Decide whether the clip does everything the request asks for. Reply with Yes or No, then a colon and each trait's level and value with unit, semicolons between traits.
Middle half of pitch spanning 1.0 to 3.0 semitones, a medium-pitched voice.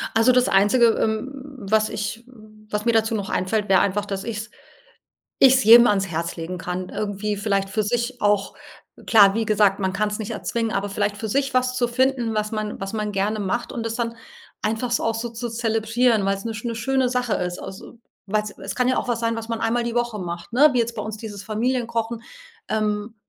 No: narrow, 2.6 semitones; high, 220 Hz